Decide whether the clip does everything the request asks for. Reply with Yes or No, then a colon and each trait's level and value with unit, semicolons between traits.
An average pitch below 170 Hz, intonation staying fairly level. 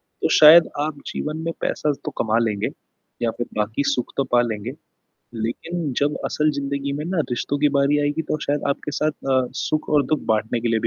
No: medium, 140 Hz; average, 4.2 semitones